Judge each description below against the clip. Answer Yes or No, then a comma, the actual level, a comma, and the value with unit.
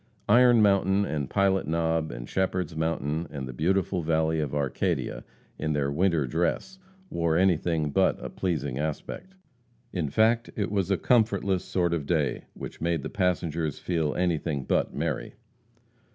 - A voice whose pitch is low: Yes, very low, 85 Hz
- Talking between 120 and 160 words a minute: Yes, average, 150 wpm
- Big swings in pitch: No, average, 4.0 semitones